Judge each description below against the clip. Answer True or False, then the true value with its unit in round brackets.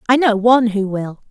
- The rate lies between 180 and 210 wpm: False (230 wpm)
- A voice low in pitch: False (220 Hz)